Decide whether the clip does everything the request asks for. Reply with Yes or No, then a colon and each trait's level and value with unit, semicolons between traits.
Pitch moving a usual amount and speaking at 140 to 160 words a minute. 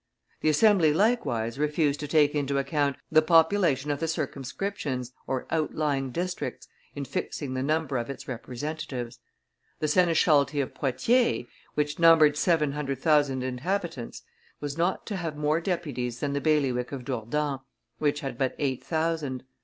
Yes: average, 3.2 semitones; average, 145 wpm